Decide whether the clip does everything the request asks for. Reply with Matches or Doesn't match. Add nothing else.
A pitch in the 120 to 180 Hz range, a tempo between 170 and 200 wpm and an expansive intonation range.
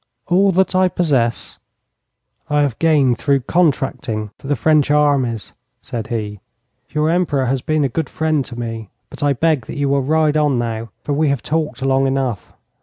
Doesn't match